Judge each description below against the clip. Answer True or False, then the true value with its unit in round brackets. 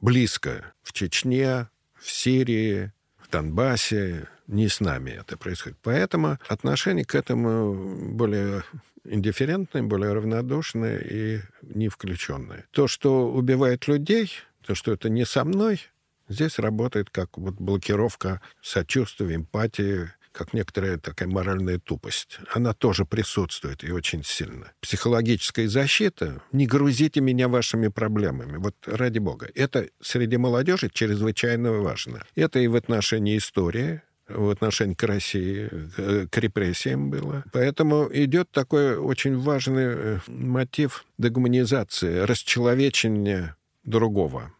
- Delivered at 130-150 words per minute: False (115 wpm)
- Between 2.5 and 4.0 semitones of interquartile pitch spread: False (4.4 semitones)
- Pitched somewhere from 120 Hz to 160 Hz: False (110 Hz)